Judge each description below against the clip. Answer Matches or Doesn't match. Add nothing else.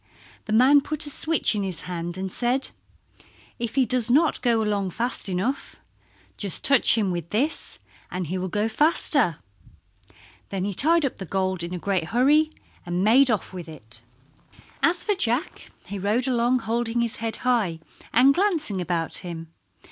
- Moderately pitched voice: Doesn't match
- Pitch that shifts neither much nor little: Doesn't match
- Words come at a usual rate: Matches